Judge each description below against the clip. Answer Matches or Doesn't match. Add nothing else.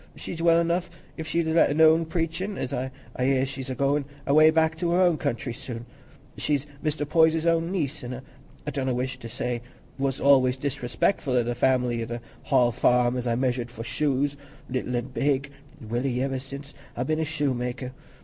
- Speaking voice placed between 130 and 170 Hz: Matches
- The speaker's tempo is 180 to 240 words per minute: Matches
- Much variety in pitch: Doesn't match